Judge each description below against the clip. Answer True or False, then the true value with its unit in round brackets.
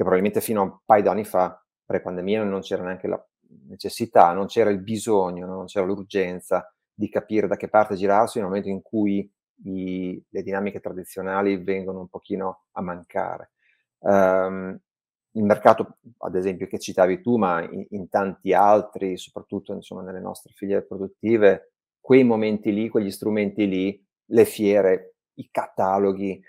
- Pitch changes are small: True (1.9 semitones)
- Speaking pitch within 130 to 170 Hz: False (100 Hz)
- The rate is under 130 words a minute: False (165 wpm)